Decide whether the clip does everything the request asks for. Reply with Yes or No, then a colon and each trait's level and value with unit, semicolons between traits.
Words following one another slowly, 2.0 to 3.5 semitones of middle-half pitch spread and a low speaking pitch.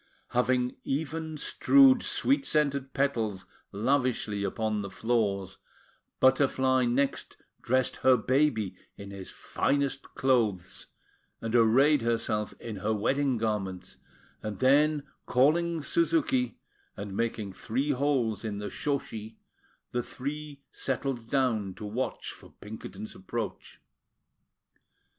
No: slow, 110 wpm; average, 4.6 semitones; low, 125 Hz